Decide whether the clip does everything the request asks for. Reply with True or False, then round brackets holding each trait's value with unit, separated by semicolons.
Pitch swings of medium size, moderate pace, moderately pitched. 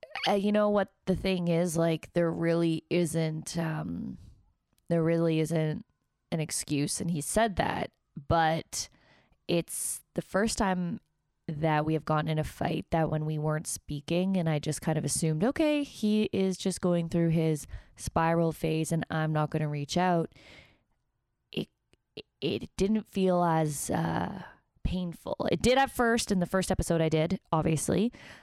True (3.2 semitones; 165 wpm; 165 Hz)